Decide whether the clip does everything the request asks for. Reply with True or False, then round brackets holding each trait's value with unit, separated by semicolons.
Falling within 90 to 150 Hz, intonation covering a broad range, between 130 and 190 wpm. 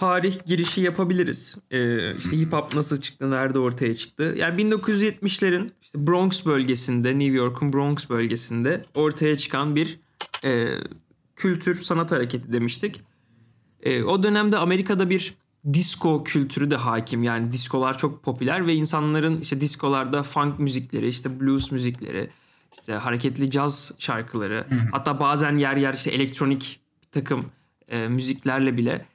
False (140 Hz; 4.1 semitones; 135 wpm)